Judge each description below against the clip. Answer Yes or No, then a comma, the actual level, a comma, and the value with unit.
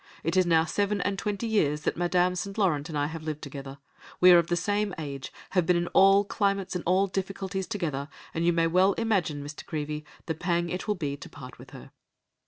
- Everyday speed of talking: No, fast, 225 wpm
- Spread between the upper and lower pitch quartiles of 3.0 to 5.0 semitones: Yes, average, 4.1 semitones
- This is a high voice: No, medium, 175 Hz